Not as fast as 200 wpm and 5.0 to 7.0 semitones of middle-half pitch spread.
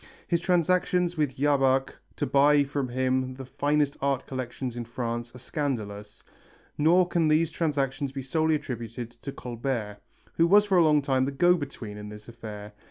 No: average, 170 wpm; average, 4.2 semitones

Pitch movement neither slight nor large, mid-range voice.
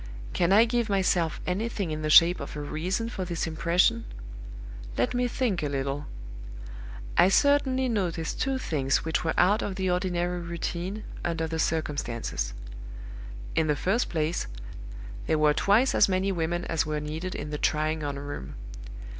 Yes: average, 4.2 semitones; medium, 170 Hz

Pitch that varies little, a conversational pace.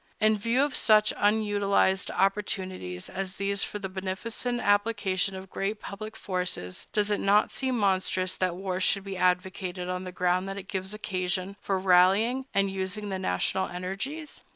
Yes: narrow, 2.0 semitones; average, 165 wpm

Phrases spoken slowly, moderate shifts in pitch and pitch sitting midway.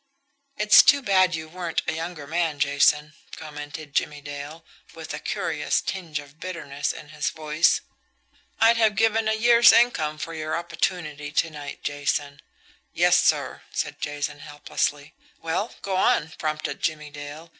No: average, 150 wpm; average, 3.5 semitones; medium, 155 Hz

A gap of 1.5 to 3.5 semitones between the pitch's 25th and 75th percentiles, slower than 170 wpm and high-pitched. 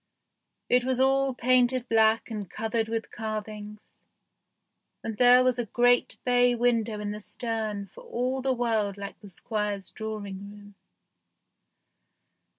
Yes: average, 2.8 semitones; slow, 135 wpm; high, 225 Hz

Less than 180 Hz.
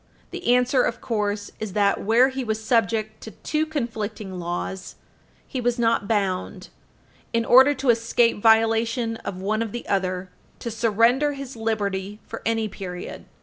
No: high, 225 Hz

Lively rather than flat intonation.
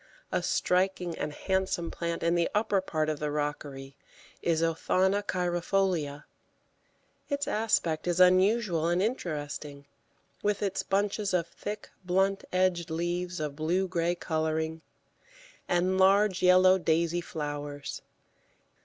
No: average, 3.1 semitones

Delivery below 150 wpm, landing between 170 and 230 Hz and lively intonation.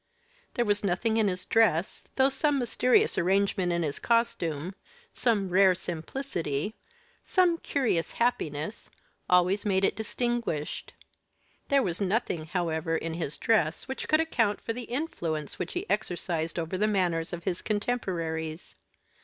Yes: average, 140 wpm; high, 190 Hz; wide, 5.9 semitones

